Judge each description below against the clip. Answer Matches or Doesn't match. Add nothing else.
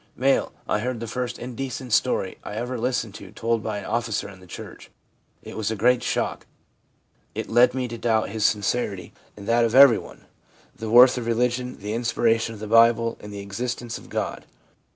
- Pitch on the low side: Matches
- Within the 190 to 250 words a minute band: Matches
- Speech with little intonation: Matches